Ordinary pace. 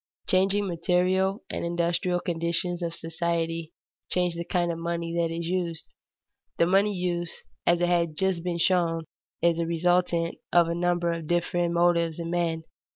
Yes: average, 160 wpm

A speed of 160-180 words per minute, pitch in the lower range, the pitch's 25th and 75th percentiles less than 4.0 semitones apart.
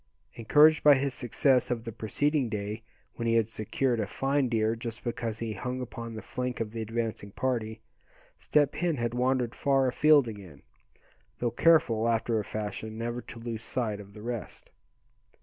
Yes: average, 175 wpm; low, 115 Hz; average, 2.7 semitones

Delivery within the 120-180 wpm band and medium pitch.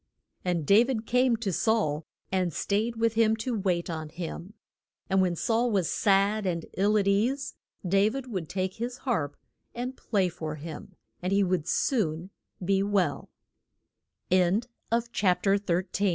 No: slow, 135 wpm; high, 200 Hz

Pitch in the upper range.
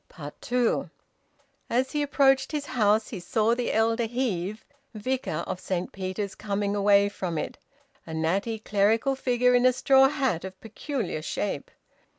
Yes: high, 220 Hz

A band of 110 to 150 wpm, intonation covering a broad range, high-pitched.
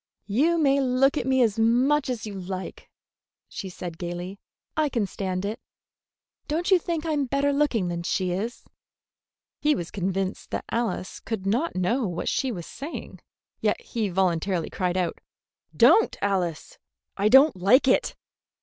No: average, 160 wpm; wide, 6.8 semitones; high, 220 Hz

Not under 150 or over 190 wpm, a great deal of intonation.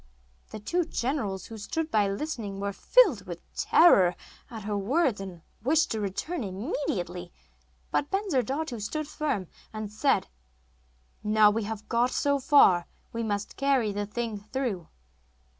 No: average, 140 wpm; wide, 5.8 semitones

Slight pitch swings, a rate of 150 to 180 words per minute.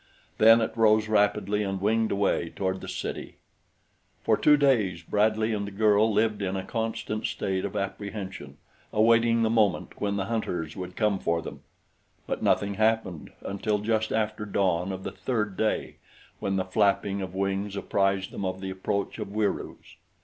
Yes: narrow, 2.2 semitones; average, 170 wpm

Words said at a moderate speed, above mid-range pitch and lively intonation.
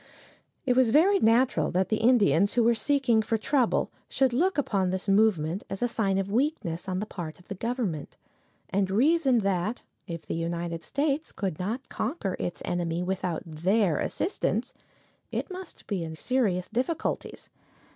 Yes: average, 165 wpm; high, 210 Hz; wide, 5.8 semitones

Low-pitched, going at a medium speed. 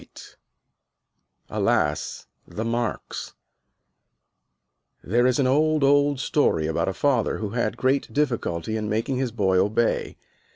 No: low, 120 Hz; slow, 125 wpm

